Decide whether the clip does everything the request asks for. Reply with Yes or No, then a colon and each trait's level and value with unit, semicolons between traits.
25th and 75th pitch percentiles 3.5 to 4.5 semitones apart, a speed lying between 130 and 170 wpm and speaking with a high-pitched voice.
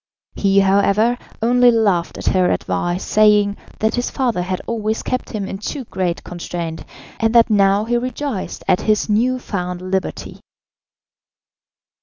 Yes: average, 3.8 semitones; average, 145 wpm; high, 210 Hz